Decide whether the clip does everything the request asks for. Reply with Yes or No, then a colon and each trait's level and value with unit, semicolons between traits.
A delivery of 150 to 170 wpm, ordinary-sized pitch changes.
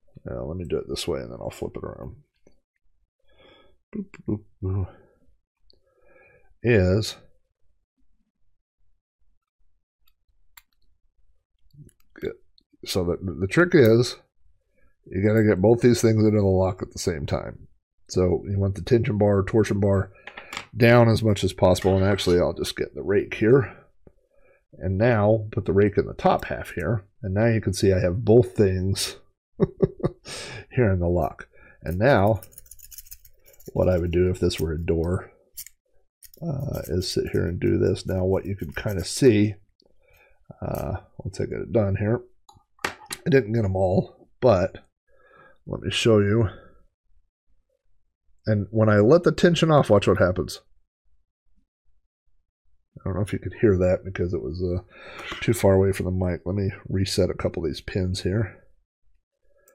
Yes: average, 160 wpm; average, 3.7 semitones